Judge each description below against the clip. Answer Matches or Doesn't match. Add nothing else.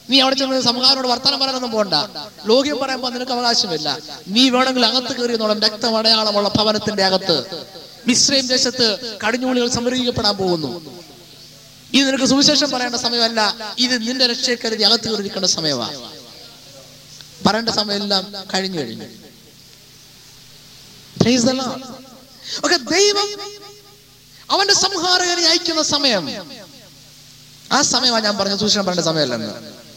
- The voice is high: Matches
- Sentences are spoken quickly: Doesn't match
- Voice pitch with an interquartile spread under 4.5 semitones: Doesn't match